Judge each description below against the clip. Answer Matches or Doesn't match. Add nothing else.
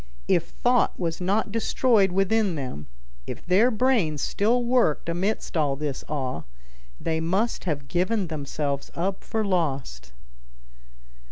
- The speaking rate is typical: Doesn't match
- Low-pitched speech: Doesn't match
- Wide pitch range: Matches